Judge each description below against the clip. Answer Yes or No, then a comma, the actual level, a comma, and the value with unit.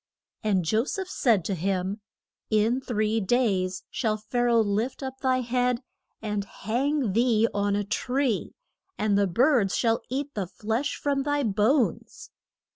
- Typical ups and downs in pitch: Yes, average, 3.9 semitones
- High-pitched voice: Yes, high, 225 Hz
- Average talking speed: Yes, average, 155 wpm